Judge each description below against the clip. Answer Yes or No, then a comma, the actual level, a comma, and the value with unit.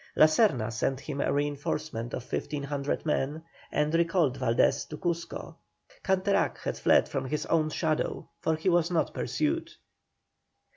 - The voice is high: No, medium, 155 Hz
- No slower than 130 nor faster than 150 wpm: Yes, average, 145 wpm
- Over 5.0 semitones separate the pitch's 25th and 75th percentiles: No, average, 3.4 semitones